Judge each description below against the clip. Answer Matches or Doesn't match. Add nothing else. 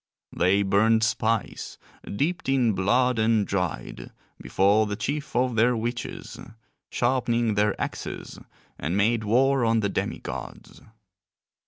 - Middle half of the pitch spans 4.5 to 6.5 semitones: Doesn't match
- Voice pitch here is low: Matches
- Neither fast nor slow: Doesn't match